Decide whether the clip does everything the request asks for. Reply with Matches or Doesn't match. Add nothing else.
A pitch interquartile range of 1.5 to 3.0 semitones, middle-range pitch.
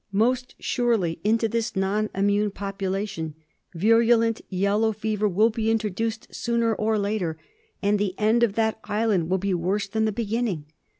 Doesn't match